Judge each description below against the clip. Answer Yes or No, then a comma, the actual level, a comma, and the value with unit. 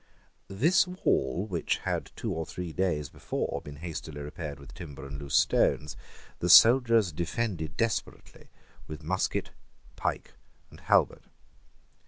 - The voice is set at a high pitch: No, very low, 85 Hz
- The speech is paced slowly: Yes, slow, 130 wpm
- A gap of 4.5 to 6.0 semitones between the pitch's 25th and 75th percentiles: Yes, average, 5.2 semitones